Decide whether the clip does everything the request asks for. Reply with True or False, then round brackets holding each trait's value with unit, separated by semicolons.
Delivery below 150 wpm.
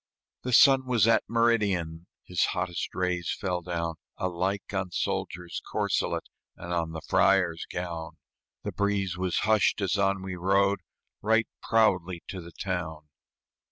True (140 wpm)